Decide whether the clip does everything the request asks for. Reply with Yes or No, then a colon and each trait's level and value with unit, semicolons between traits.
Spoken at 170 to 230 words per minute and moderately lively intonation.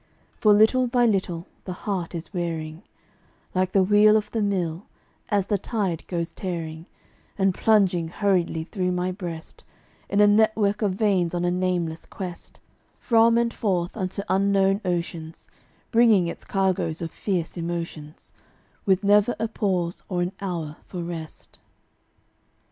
No: average, 145 wpm; average, 3.2 semitones